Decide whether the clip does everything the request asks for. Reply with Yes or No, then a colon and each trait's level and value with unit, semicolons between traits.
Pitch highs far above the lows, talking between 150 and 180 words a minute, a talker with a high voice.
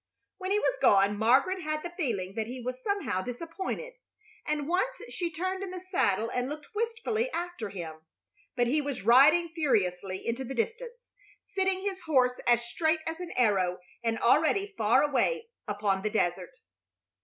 Yes: wide, 8.7 semitones; average, 165 wpm; very high, 295 Hz